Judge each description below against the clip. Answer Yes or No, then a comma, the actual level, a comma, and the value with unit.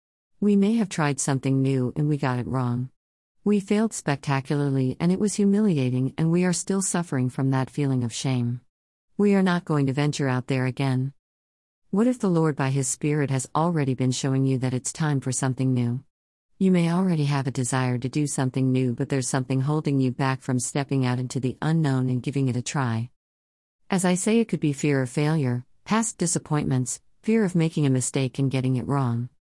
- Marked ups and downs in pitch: No, average, 3.6 semitones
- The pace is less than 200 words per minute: No, fast, 205 wpm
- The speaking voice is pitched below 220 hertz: Yes, low, 135 Hz